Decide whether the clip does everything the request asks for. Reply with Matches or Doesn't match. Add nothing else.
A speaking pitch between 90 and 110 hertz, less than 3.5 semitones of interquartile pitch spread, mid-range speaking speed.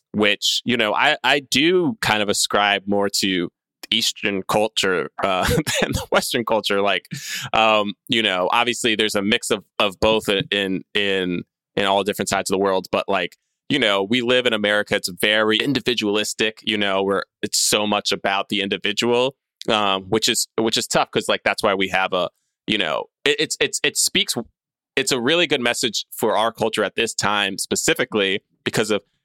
Matches